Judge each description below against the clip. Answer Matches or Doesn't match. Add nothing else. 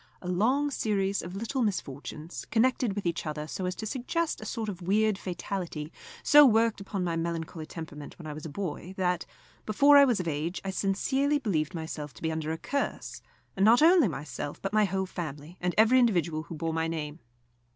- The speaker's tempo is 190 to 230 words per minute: Matches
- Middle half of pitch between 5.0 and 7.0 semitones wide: Matches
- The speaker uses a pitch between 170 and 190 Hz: Matches